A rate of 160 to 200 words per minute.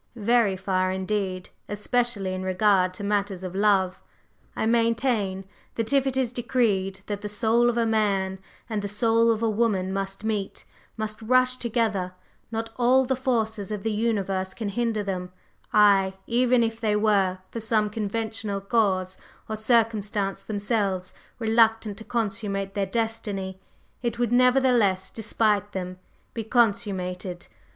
No: average, 145 wpm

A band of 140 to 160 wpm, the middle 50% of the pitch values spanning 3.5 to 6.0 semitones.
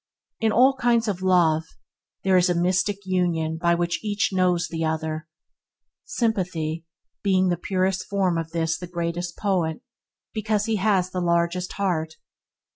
No: average, 150 wpm; average, 2.7 semitones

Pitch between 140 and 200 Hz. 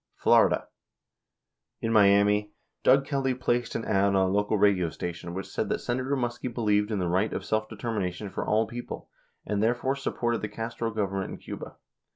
No: low, 105 Hz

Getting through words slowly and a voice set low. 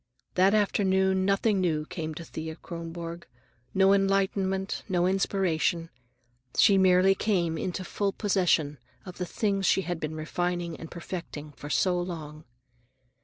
No: slow, 130 wpm; medium, 180 Hz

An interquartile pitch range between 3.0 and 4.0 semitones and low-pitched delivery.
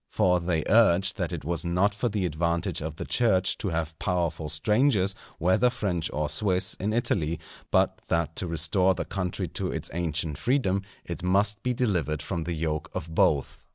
Yes: average, 3.5 semitones; very low, 90 Hz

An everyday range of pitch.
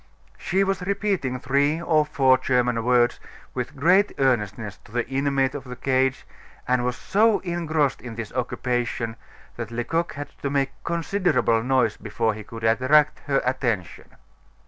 Yes: average, 4.0 semitones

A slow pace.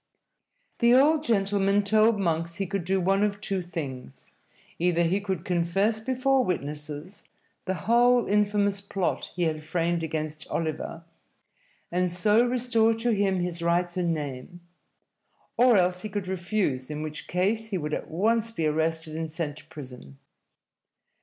No: average, 155 wpm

